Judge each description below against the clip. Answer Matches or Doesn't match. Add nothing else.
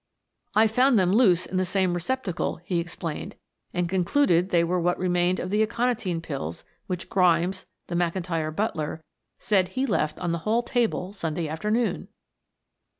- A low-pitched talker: Doesn't match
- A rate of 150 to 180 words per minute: Matches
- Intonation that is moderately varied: Matches